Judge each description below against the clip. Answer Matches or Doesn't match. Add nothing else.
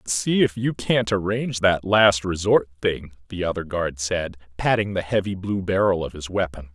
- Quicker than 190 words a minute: Doesn't match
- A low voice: Matches